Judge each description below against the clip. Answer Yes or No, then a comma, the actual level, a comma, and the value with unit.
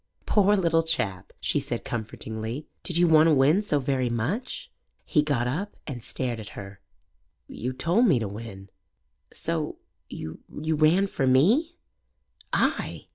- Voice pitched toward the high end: No, medium, 140 Hz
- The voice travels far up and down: Yes, wide, 6.7 semitones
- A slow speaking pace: No, average, 145 wpm